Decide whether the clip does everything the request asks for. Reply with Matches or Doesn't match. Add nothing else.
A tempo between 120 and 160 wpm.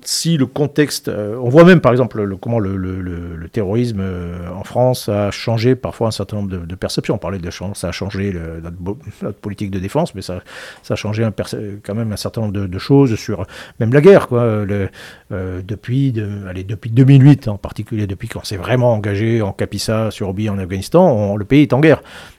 Doesn't match